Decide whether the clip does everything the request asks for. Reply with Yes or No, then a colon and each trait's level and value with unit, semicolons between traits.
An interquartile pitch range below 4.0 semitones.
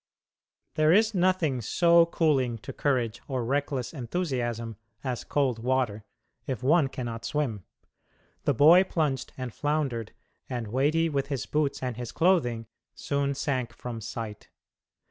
No: average, 4.3 semitones